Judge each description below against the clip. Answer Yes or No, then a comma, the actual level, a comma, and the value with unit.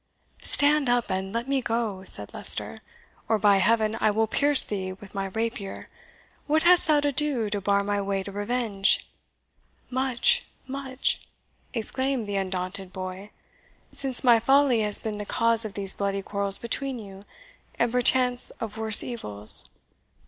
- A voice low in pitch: No, high, 220 Hz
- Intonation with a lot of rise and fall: No, average, 4.3 semitones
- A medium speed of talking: Yes, average, 155 wpm